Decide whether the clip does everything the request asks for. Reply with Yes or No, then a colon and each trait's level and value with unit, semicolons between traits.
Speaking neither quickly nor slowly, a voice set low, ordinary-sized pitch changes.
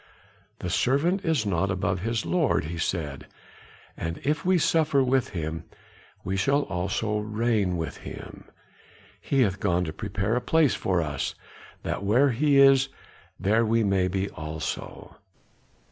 No: average, 145 wpm; low, 105 Hz; wide, 6.9 semitones